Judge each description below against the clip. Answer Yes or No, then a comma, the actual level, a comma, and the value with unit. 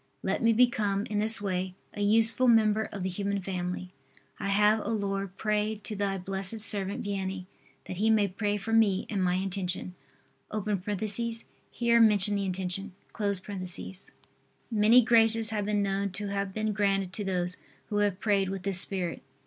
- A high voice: Yes, high, 200 Hz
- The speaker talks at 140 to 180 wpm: Yes, average, 165 wpm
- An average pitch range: No, narrow, 1.9 semitones